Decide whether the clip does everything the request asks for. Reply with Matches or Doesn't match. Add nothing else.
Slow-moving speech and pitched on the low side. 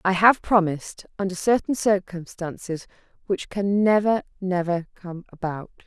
Doesn't match